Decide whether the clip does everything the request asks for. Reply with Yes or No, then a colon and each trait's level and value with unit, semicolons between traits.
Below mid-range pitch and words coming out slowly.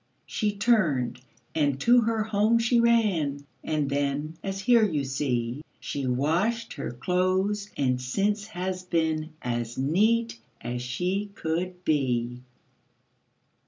No: medium, 165 Hz; slow, 125 wpm